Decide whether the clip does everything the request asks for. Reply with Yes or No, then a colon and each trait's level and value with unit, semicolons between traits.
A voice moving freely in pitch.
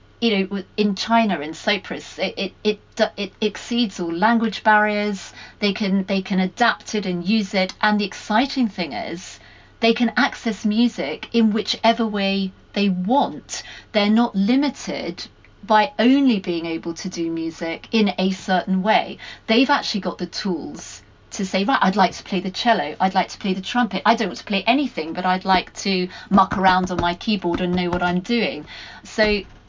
No: average, 3.4 semitones